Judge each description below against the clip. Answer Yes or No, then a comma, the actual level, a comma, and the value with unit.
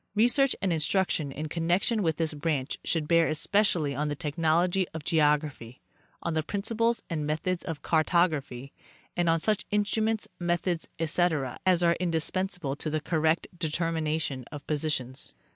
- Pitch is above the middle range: No, medium, 165 Hz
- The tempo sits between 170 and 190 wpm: No, average, 155 wpm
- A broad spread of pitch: No, average, 2.9 semitones